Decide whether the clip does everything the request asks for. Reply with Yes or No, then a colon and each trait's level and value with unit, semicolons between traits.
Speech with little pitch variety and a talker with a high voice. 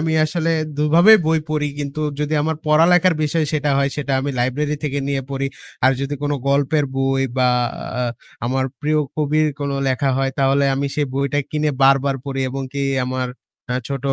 No: narrow, 2.1 semitones; medium, 140 Hz